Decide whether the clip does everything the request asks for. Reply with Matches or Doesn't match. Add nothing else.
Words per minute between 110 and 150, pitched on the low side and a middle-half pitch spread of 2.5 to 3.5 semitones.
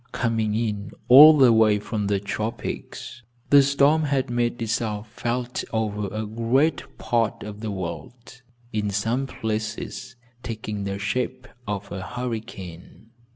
Matches